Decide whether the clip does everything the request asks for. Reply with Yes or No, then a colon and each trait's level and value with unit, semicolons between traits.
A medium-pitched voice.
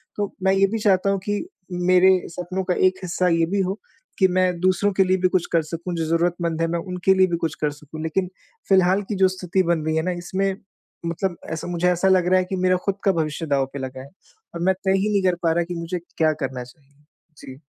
Yes: medium, 180 Hz